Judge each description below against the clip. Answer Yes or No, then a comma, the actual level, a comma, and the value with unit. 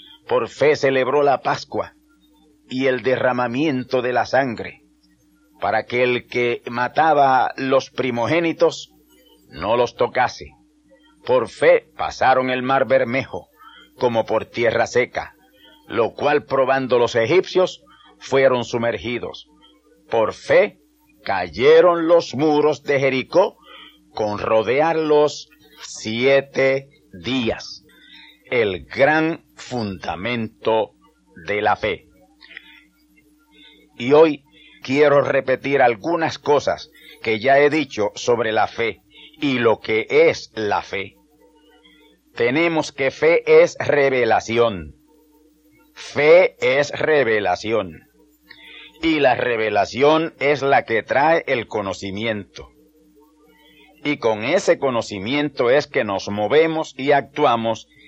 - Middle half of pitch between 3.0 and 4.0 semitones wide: Yes, average, 3.6 semitones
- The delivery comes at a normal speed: No, slow, 105 wpm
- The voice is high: No, medium, 145 Hz